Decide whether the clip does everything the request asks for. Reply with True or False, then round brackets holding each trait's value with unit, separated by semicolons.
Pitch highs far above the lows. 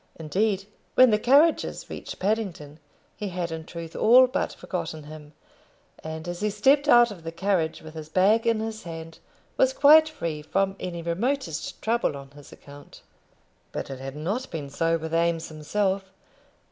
True (5.7 semitones)